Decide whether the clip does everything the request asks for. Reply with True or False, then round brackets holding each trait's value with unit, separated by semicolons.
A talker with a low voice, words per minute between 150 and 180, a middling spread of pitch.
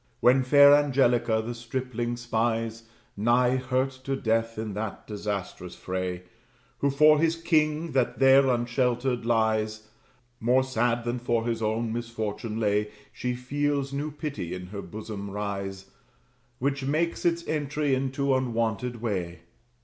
False (120 Hz; 135 wpm; 3.5 semitones)